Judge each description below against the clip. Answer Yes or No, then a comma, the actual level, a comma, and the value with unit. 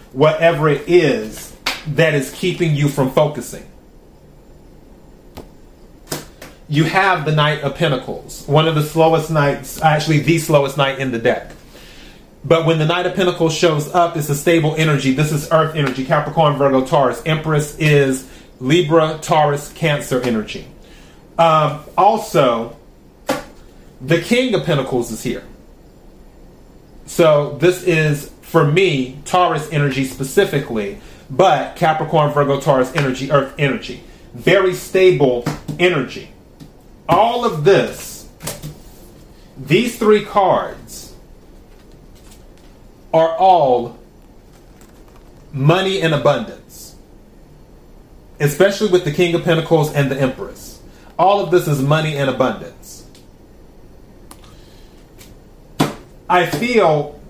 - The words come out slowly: Yes, slow, 110 wpm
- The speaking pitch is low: No, medium, 155 Hz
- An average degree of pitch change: Yes, average, 3.1 semitones